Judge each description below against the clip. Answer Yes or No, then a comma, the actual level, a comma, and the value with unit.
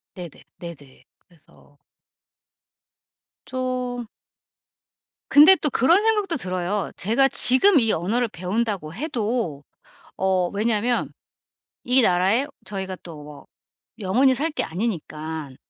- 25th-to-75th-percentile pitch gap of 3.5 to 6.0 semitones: No, wide, 6.5 semitones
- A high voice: Yes, high, 210 Hz